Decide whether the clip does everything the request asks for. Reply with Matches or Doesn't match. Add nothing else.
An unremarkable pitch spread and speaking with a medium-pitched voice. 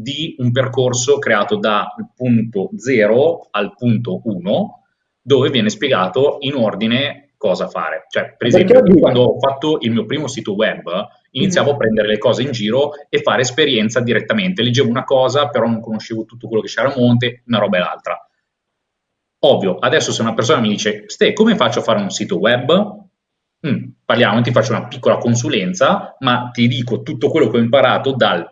Doesn't match